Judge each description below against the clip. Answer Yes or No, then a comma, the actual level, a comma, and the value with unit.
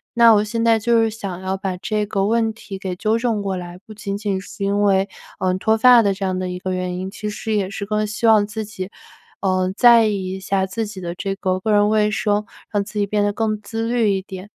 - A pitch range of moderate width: No, narrow, 2.3 semitones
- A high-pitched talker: Yes, high, 205 Hz